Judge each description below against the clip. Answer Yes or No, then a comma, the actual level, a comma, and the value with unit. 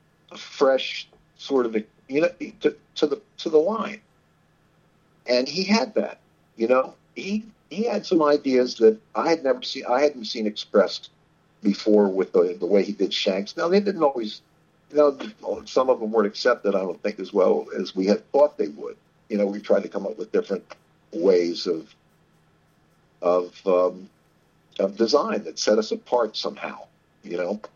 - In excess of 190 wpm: No, average, 180 wpm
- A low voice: No, medium, 145 Hz